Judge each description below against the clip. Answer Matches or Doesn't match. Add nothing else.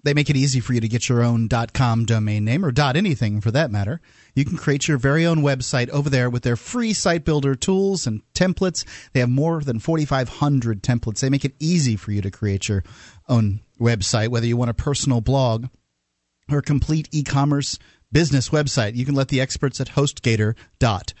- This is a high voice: Doesn't match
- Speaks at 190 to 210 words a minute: Matches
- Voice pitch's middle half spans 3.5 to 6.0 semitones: Matches